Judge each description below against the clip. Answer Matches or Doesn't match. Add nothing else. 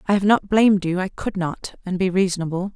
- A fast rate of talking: Matches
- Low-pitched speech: Doesn't match